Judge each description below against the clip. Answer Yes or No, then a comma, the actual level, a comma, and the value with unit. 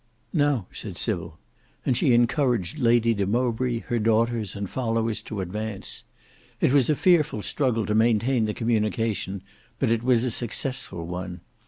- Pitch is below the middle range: Yes, low, 115 Hz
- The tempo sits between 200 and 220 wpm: No, average, 155 wpm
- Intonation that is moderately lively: Yes, average, 3.0 semitones